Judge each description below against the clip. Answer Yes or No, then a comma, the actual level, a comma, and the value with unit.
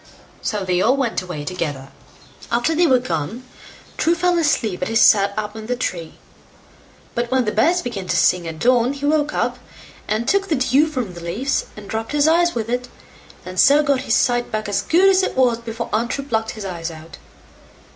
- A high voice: Yes, high, 235 Hz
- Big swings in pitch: Yes, wide, 6.0 semitones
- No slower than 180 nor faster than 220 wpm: Yes, fast, 205 wpm